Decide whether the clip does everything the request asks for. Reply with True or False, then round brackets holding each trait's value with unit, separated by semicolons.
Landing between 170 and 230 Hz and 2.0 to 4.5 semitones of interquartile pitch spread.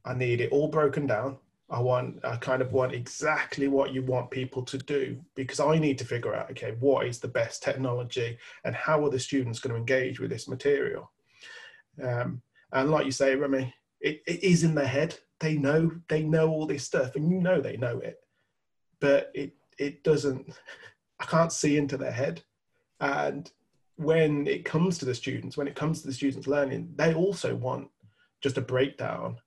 False (140 Hz; 3.0 semitones)